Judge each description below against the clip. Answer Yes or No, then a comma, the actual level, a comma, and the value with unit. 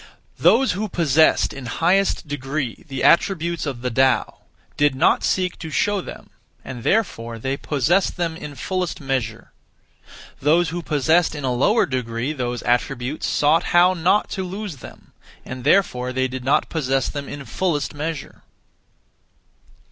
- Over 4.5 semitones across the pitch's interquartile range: Yes, average, 5.1 semitones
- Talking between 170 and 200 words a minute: No, average, 150 wpm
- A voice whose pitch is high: No, medium, 145 Hz